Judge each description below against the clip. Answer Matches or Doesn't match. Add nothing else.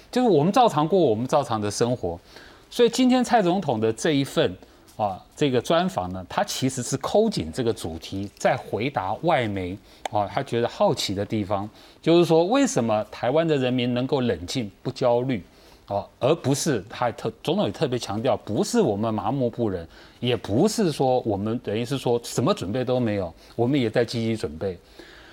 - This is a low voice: Matches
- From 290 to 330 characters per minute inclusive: Doesn't match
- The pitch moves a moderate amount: Doesn't match